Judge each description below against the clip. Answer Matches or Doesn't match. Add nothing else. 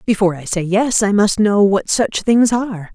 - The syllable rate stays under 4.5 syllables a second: Doesn't match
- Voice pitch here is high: Matches